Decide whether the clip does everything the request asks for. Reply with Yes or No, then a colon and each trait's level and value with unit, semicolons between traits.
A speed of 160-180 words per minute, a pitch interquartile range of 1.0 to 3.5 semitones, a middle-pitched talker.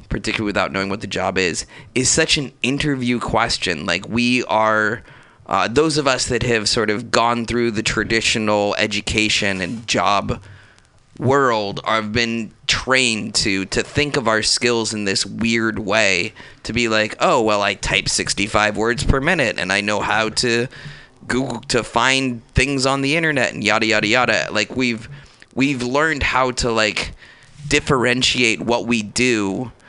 No: average, 165 wpm; average, 3.0 semitones; low, 115 Hz